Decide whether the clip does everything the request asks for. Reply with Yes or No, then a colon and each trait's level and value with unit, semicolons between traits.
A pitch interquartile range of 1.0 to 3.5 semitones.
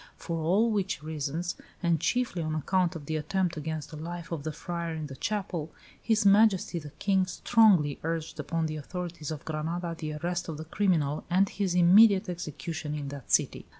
Yes: average, 3.1 semitones